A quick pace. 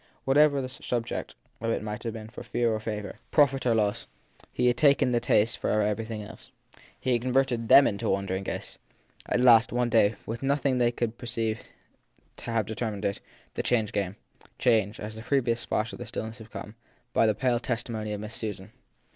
Yes: fast, 215 wpm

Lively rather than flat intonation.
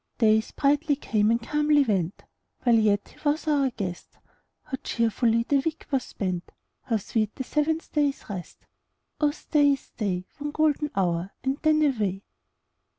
Yes: wide, 5.9 semitones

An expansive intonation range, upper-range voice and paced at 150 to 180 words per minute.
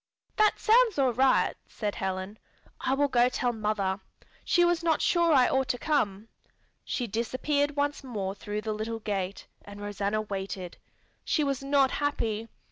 Yes: wide, 5.8 semitones; high, 240 Hz; average, 165 wpm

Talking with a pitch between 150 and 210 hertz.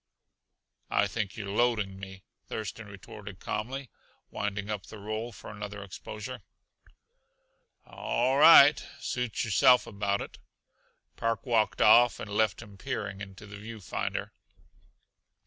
No: low, 105 Hz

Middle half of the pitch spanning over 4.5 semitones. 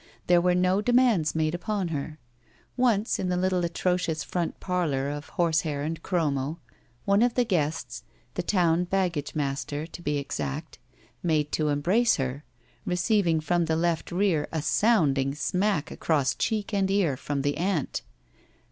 No: average, 4.0 semitones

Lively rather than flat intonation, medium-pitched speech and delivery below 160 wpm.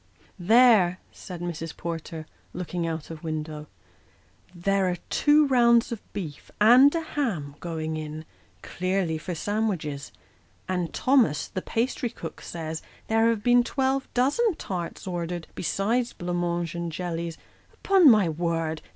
Yes: wide, 6.0 semitones; medium, 180 Hz; average, 140 wpm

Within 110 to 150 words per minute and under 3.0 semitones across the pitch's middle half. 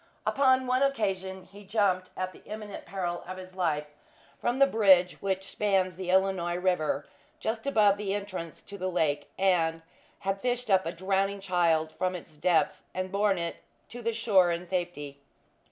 No: average, 175 wpm; narrow, 2.5 semitones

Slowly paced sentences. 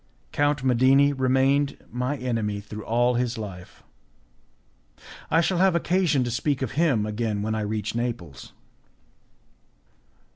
Yes: slow, 125 wpm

